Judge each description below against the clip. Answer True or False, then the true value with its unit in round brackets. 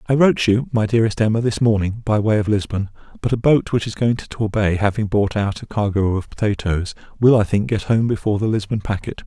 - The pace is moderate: False (235 wpm)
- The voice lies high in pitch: False (105 Hz)